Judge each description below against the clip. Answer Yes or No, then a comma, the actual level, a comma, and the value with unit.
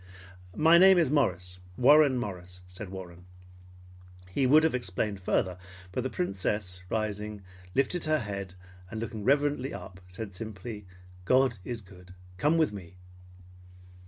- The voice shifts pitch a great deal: Yes, wide, 6.7 semitones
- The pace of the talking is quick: No, slow, 135 wpm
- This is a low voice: Yes, low, 105 Hz